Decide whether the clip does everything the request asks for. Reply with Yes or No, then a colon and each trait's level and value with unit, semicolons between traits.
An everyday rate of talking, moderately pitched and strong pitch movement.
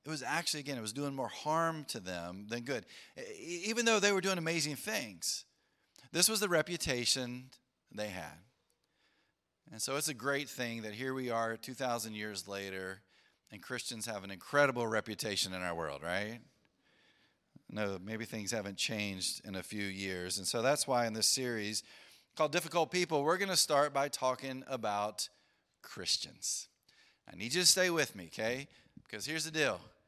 No: average, 175 wpm; low, 120 Hz; wide, 6.2 semitones